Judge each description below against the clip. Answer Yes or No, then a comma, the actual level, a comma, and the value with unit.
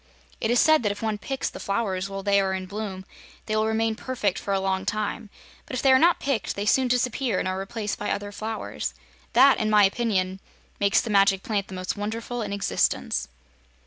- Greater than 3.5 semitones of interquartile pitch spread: No, average, 2.9 semitones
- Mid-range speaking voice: No, high, 210 Hz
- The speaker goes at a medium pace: No, fast, 215 wpm